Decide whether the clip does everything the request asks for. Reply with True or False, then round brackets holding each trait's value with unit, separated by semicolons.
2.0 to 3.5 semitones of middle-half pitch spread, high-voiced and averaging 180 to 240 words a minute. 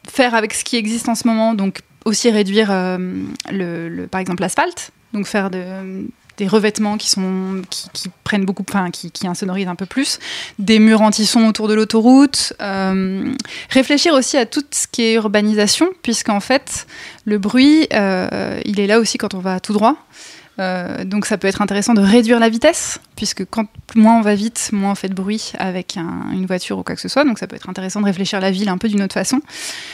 True (3.2 semitones; 210 Hz; 220 wpm)